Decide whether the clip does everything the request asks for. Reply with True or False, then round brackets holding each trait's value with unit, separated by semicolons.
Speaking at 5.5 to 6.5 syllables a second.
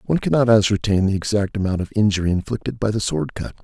False (6.7 syllables/s)